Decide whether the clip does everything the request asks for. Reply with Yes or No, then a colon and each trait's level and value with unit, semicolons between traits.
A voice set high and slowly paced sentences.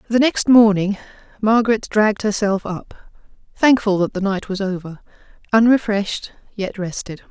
Yes: high, 205 Hz; slow, 125 wpm